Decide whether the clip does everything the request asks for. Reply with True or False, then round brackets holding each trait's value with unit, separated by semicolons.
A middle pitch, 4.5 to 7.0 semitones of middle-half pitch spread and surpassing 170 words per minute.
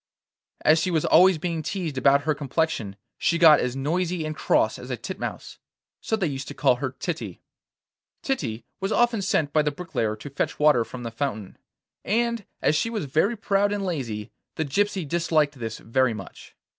True (155 Hz; 5.5 semitones; 185 wpm)